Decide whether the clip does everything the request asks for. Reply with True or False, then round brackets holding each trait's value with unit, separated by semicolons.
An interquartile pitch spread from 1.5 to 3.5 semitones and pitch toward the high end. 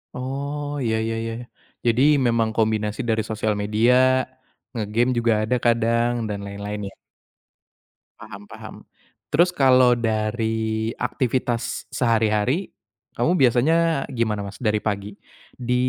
False (2.5 semitones; 115 Hz)